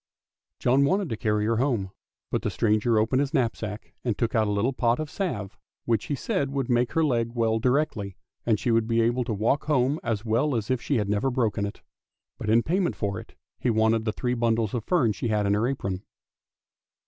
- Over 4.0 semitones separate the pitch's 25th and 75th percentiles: No, average, 3.3 semitones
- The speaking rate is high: Yes, fast, 220 wpm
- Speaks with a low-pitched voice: Yes, low, 115 Hz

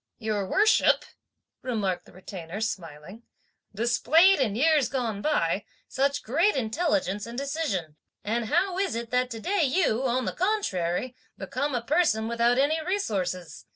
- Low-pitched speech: No, high, 240 Hz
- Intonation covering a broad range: Yes, wide, 6.9 semitones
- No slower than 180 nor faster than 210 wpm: No, average, 140 wpm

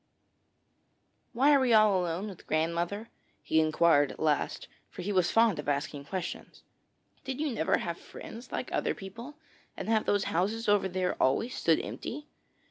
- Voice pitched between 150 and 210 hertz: Yes, high, 190 Hz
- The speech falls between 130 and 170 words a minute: Yes, average, 165 wpm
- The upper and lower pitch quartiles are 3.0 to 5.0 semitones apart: No, wide, 5.6 semitones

